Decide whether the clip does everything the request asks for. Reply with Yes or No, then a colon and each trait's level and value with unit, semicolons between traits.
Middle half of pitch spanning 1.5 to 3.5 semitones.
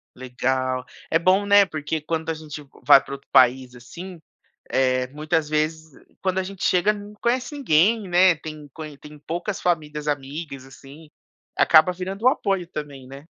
No: average, 4.6 semitones